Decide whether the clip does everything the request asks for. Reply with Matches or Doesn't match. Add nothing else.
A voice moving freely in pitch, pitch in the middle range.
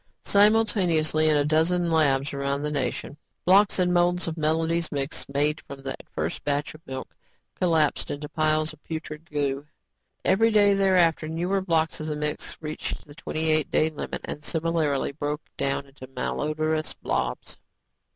Doesn't match